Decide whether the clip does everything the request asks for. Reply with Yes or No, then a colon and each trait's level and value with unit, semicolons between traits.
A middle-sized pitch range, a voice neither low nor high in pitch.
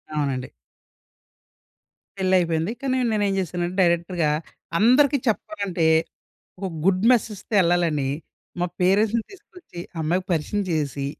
Yes: average, 4.2 semitones; medium, 180 Hz